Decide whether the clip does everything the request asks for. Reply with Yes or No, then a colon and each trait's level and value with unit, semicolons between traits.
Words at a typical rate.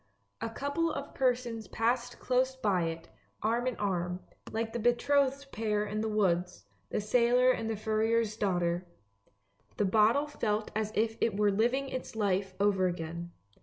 Yes: average, 160 wpm